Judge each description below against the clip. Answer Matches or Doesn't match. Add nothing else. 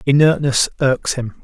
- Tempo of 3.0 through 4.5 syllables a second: Matches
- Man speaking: Matches